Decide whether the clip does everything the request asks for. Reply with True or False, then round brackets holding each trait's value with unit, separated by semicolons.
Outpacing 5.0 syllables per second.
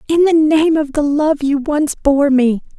False (4.0 syllables/s)